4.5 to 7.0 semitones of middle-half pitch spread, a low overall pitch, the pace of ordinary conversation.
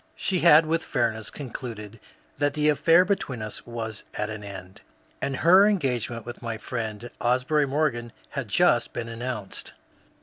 Yes: average, 5.2 semitones; low, 120 Hz; average, 155 wpm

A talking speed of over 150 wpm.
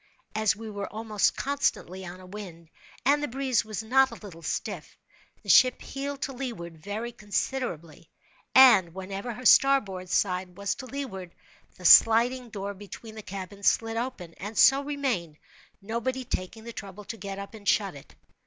Yes: average, 170 wpm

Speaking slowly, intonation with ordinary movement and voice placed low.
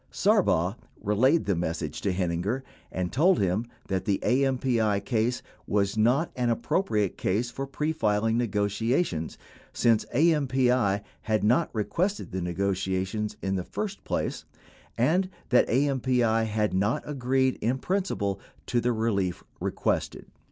Yes: slow, 130 wpm; average, 4.9 semitones; low, 115 Hz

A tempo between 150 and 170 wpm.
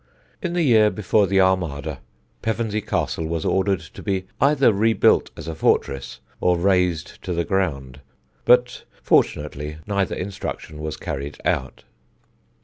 No: average, 140 wpm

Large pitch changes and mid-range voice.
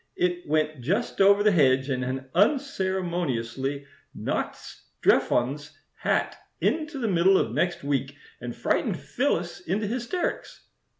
Yes: wide, 6.8 semitones; medium, 170 Hz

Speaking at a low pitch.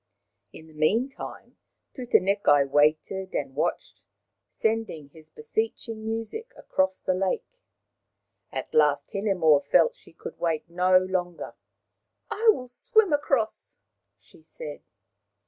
No: high, 190 Hz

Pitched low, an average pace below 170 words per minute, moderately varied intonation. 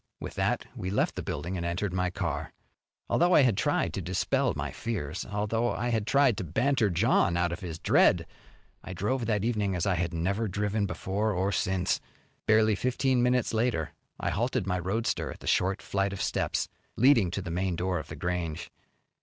No: low, 100 Hz; average, 195 wpm; average, 4.2 semitones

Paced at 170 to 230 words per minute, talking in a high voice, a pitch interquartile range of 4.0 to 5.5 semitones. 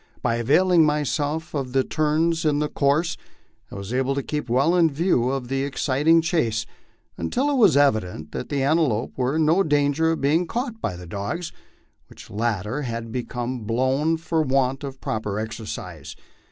No: average, 175 wpm; medium, 140 Hz; average, 5.2 semitones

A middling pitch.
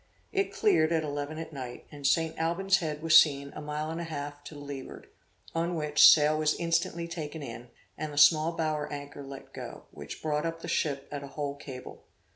Yes: medium, 150 Hz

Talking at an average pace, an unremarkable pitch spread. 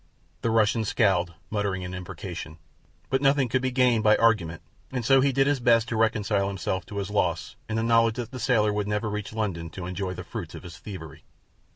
No: fast, 215 wpm; average, 3.9 semitones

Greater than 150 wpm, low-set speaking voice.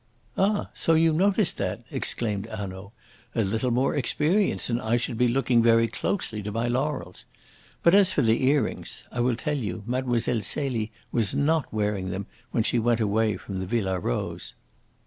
Yes: average, 175 wpm; low, 120 Hz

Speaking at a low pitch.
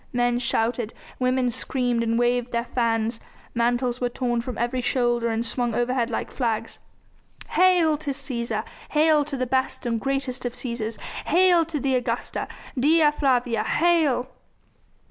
No: high, 245 Hz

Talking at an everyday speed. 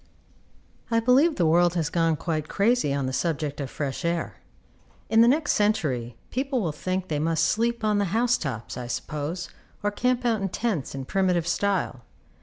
Yes: average, 190 wpm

